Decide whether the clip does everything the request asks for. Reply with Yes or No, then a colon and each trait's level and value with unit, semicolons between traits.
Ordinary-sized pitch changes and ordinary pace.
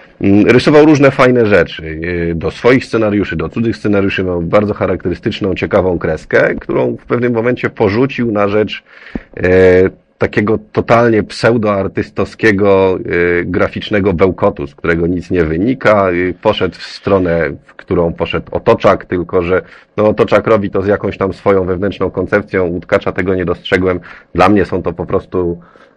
Yes: average, 3.1 semitones; average, 140 wpm